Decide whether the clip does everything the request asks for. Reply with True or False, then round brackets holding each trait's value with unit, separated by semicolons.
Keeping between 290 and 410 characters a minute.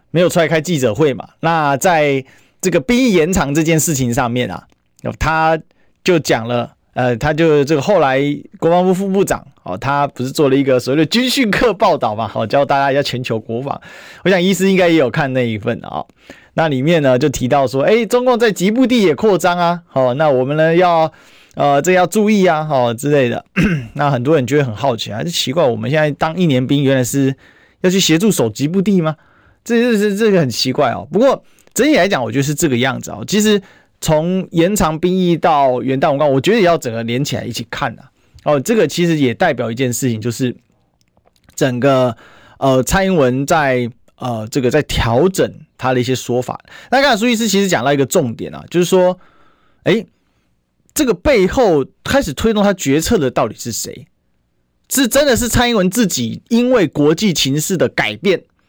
True (295 characters per minute)